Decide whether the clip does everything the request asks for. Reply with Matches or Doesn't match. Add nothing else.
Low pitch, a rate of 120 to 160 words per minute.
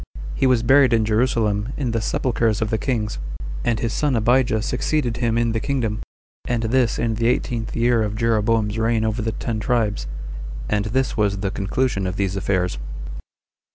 Doesn't match